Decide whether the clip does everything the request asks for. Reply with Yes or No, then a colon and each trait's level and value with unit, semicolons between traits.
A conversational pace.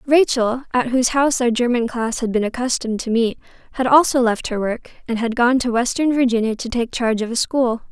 No: fast, 220 wpm